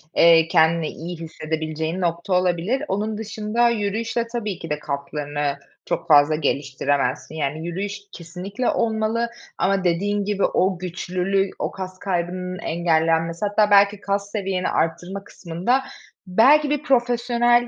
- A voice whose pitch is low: No, medium, 185 Hz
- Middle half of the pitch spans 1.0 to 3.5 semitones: No, average, 4.4 semitones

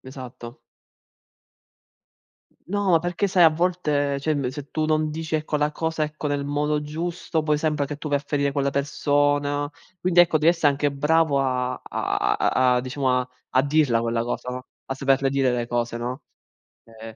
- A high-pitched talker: No, medium, 145 Hz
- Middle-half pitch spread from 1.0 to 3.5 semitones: Yes, average, 2.8 semitones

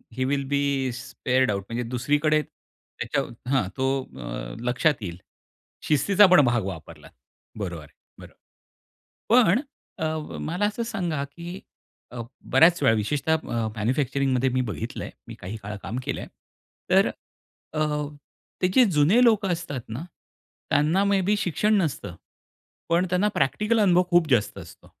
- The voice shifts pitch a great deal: Yes, wide, 6.4 semitones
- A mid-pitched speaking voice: Yes, medium, 145 Hz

